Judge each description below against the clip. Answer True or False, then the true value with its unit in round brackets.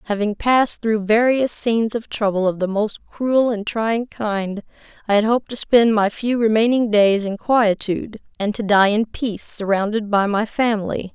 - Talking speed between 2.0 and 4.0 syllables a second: False (4.8 syllables/s)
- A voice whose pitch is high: True (215 Hz)